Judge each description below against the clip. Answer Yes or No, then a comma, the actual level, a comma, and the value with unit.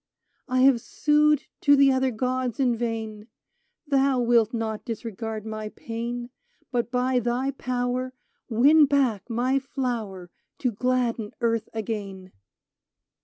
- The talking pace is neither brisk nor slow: No, slow, 120 wpm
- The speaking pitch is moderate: No, high, 240 Hz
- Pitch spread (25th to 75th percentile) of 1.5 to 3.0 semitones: Yes, average, 2.7 semitones